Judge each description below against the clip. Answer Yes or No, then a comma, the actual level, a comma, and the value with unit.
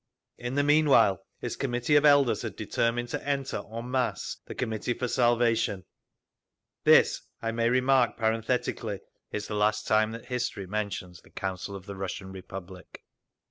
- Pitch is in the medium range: No, low, 115 Hz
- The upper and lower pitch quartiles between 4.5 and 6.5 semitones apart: No, average, 3.8 semitones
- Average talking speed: Yes, average, 150 wpm